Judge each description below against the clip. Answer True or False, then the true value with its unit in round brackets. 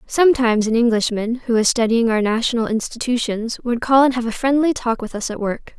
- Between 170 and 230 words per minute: True (205 wpm)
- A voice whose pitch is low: False (235 Hz)